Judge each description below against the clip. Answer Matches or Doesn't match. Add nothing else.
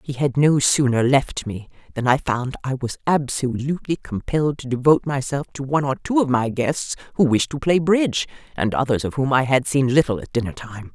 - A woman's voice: Matches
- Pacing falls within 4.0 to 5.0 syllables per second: Doesn't match